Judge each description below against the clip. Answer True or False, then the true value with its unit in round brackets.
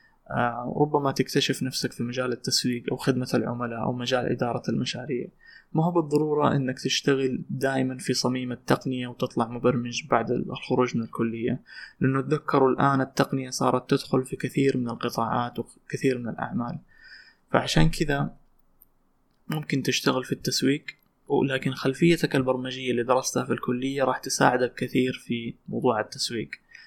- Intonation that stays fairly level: True (1.9 semitones)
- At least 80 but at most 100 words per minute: False (135 wpm)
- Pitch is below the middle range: True (130 Hz)